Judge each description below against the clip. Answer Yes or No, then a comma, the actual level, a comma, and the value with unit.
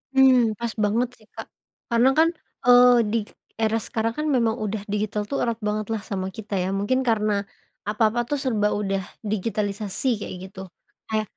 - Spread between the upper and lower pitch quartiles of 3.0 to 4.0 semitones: No, narrow, 2.4 semitones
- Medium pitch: No, high, 220 Hz